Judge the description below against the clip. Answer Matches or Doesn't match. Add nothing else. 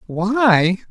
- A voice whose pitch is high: Matches